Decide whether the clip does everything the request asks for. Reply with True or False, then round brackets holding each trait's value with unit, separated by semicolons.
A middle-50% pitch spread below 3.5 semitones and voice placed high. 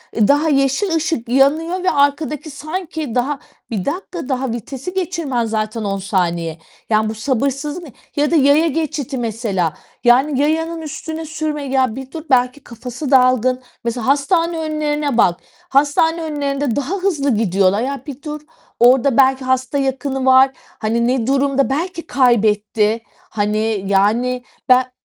False (4.3 semitones; 270 Hz)